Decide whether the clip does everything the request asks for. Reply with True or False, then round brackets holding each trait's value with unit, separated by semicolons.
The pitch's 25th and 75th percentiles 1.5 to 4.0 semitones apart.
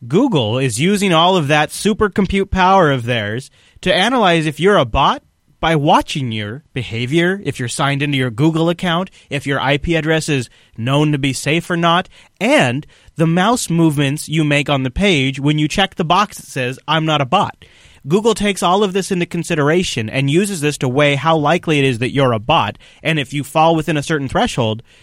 False (4.7 semitones)